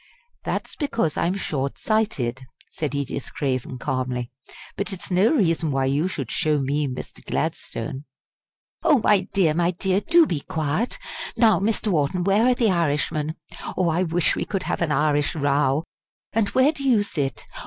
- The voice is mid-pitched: Yes, medium, 165 Hz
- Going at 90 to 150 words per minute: No, average, 165 wpm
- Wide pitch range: Yes, wide, 6.1 semitones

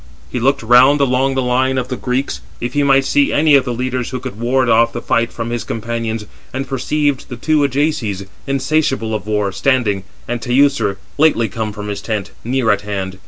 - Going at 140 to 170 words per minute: No, fast, 205 wpm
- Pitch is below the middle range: Yes, low, 125 Hz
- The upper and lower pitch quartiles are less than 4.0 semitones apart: Yes, average, 3.3 semitones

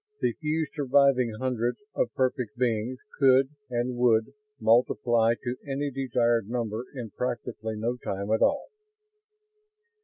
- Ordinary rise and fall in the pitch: No, narrow, 2.3 semitones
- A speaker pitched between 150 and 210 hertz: No, low, 120 Hz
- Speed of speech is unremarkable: No, slow, 125 wpm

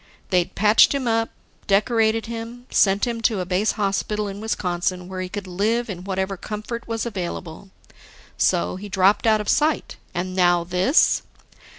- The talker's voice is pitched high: Yes, high, 200 Hz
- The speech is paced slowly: No, average, 165 wpm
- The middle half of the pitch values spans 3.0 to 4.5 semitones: Yes, average, 3.5 semitones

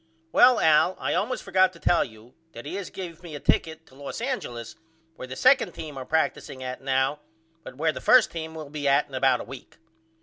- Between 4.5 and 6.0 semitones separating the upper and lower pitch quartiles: Yes, average, 4.9 semitones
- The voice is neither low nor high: Yes, medium, 150 Hz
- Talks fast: Yes, fast, 225 wpm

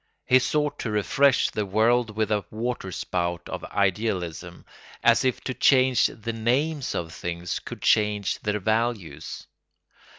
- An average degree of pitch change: Yes, average, 4.5 semitones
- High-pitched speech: No, low, 110 Hz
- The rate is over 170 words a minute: No, average, 140 wpm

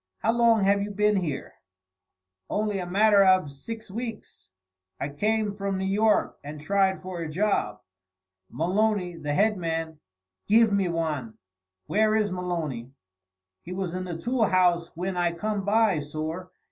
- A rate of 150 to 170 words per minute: Yes, average, 155 wpm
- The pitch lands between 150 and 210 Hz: Yes, high, 190 Hz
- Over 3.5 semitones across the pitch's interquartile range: Yes, average, 4.1 semitones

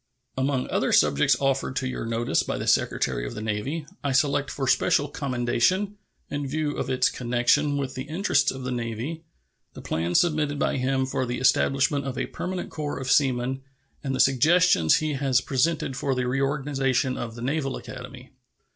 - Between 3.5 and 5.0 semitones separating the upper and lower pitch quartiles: No, narrow, 2.4 semitones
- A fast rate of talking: No, average, 180 wpm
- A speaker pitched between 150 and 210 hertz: No, low, 135 Hz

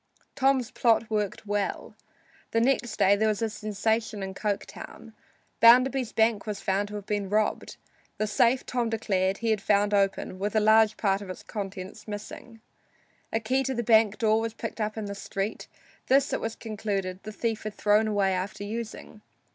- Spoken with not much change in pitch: Yes, narrow, 2.0 semitones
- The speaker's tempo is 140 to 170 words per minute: No, average, 180 wpm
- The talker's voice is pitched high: Yes, high, 215 Hz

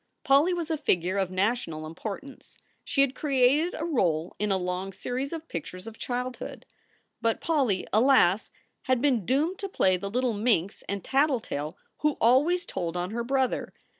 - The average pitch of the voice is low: No, high, 245 Hz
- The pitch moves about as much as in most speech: No, wide, 6.7 semitones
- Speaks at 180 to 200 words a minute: No, average, 165 wpm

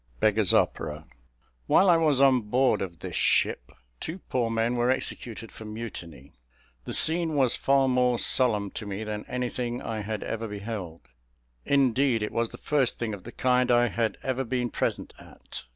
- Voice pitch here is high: No, low, 120 Hz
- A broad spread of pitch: No, average, 3.3 semitones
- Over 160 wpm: Yes, average, 175 wpm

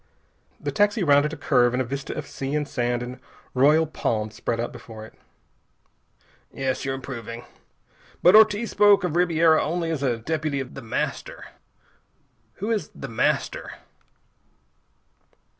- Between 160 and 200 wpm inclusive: No, average, 145 wpm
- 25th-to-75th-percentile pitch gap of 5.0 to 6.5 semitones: Yes, wide, 5.5 semitones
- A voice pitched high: No, medium, 140 Hz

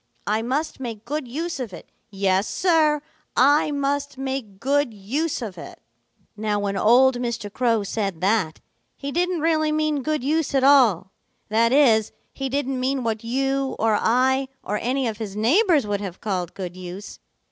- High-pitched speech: Yes, very high, 250 Hz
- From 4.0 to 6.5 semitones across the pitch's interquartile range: Yes, average, 5.3 semitones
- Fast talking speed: No, average, 170 wpm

